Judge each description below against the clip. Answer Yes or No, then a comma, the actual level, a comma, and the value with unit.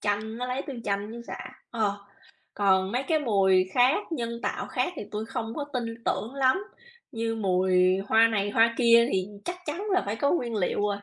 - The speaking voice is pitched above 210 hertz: Yes, high, 225 Hz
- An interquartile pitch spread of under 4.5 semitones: Yes, average, 3.8 semitones